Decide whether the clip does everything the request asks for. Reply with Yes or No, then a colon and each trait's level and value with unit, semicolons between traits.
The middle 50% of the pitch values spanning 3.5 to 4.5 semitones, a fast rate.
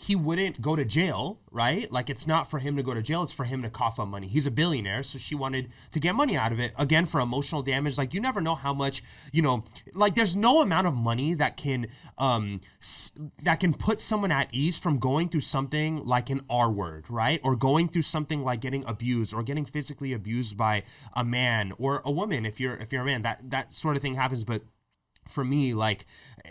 Yes: average, 4.1 semitones; fast, 235 wpm